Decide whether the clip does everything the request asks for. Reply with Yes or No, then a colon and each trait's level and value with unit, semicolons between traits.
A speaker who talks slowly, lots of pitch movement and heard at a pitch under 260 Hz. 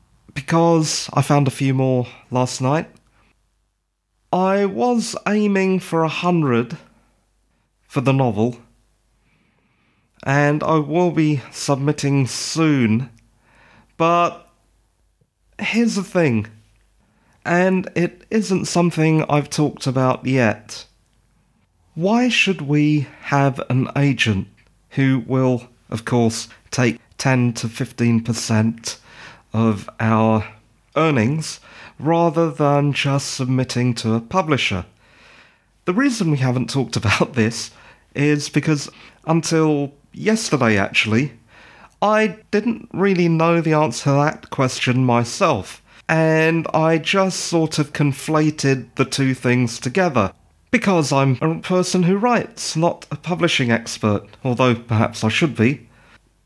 Yes: slow, 115 wpm; wide, 5.8 semitones; medium, 140 Hz